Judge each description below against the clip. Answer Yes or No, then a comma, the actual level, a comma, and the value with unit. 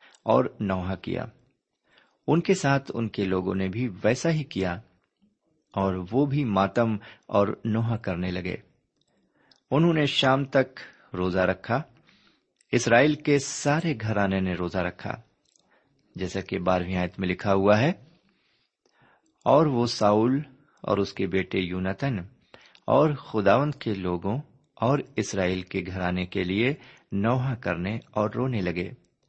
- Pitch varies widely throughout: Yes, wide, 6.1 semitones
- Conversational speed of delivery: Yes, average, 135 wpm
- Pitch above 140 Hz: No, low, 110 Hz